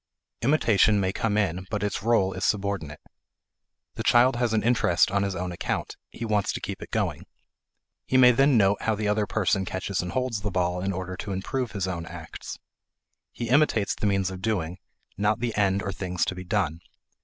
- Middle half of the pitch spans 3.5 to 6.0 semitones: No, average, 3.1 semitones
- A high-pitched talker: No, low, 100 Hz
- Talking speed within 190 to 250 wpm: Yes, average, 200 wpm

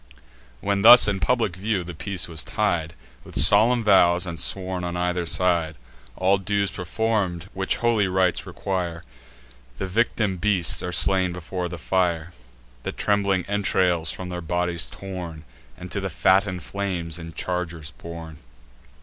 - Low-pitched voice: Yes, very low, 90 Hz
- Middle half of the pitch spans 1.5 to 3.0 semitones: Yes, narrow, 2.5 semitones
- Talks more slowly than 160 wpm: Yes, average, 150 wpm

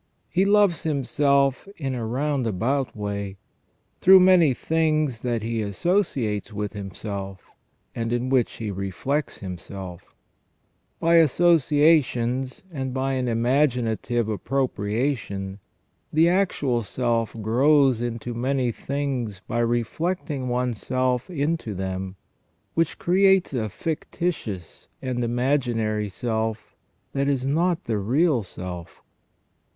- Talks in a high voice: No, low, 125 Hz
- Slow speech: Yes, slow, 115 wpm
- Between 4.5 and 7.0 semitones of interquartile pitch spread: Yes, average, 5.0 semitones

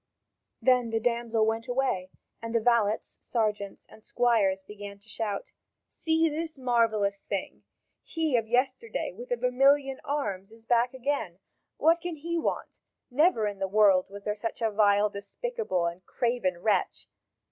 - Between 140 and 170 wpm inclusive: Yes, average, 155 wpm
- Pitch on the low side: No, high, 230 Hz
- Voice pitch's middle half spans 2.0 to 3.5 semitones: No, average, 4.9 semitones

